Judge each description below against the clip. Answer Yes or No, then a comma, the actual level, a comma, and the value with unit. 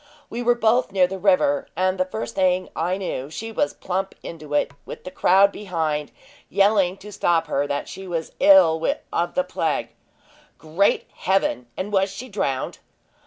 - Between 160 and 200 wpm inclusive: Yes, average, 170 wpm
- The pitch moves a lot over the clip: No, average, 3.8 semitones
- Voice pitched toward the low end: No, medium, 185 Hz